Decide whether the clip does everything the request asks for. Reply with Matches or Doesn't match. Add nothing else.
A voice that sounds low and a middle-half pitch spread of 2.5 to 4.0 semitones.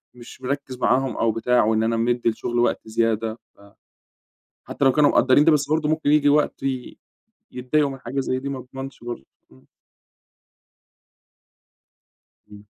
Matches